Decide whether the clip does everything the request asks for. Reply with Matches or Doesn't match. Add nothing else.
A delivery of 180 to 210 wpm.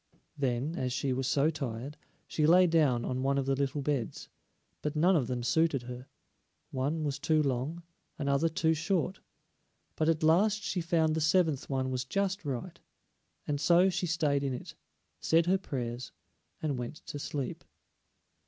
Doesn't match